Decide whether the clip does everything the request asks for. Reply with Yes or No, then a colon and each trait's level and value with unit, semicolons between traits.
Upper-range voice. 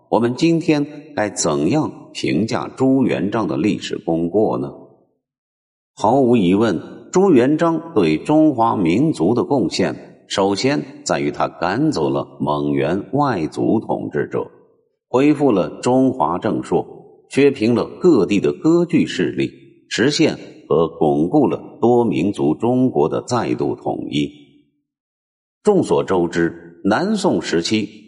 No: low, 115 Hz